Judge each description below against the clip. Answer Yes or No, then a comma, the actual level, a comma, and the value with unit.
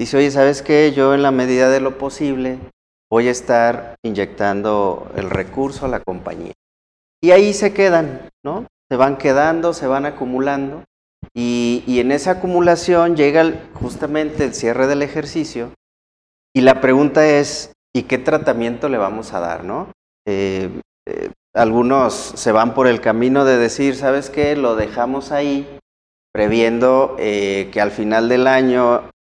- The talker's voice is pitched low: Yes, low, 130 Hz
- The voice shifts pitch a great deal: No, average, 3.9 semitones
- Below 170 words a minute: Yes, average, 155 wpm